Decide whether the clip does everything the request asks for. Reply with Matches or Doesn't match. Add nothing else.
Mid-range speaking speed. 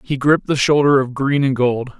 Doesn't match